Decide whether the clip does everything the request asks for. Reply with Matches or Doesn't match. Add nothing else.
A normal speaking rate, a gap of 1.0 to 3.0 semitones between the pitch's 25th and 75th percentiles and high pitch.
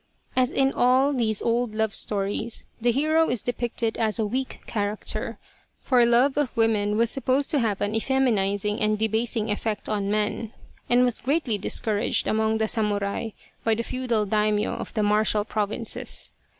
Matches